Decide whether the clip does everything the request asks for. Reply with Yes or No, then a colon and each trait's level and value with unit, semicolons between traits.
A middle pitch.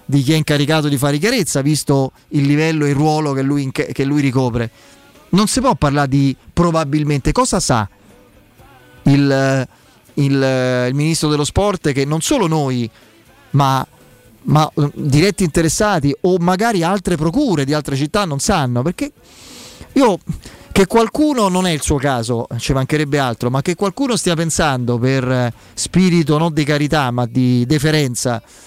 Yes: medium, 145 Hz